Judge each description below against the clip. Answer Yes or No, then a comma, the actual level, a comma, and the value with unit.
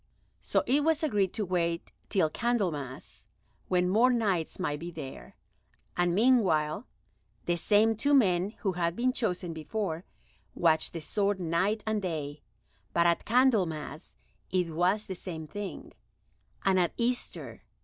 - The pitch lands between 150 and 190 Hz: Yes, medium, 185 Hz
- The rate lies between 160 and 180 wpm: No, average, 140 wpm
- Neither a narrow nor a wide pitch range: Yes, average, 4.5 semitones